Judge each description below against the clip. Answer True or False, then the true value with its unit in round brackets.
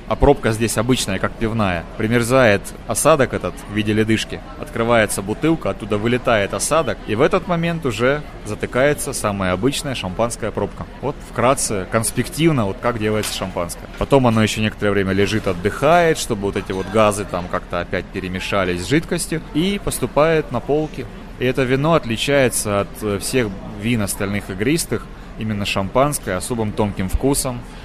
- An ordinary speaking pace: True (150 wpm)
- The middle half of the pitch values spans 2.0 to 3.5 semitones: False (4.7 semitones)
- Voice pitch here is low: True (110 Hz)